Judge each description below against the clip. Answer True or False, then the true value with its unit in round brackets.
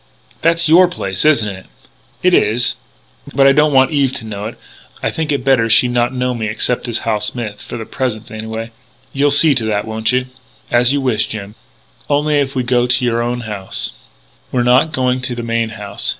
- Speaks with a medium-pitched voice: False (120 Hz)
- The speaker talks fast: True (215 wpm)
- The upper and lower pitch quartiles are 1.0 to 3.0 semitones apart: False (3.5 semitones)